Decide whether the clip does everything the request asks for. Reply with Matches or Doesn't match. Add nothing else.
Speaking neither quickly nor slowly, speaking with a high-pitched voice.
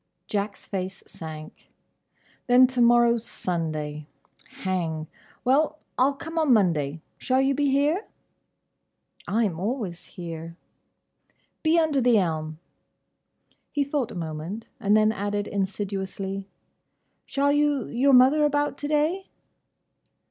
Doesn't match